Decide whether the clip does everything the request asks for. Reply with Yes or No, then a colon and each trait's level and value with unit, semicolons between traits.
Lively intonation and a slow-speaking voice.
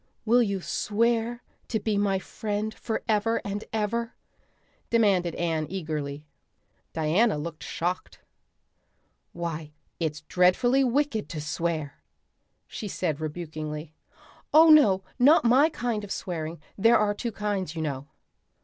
Yes: wide, 6.1 semitones; slow, 120 wpm